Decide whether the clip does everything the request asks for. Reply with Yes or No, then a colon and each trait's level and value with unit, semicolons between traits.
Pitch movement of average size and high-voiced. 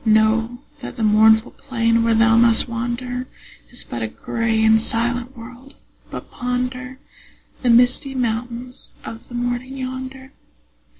No: narrow, 1.8 semitones; high, 240 Hz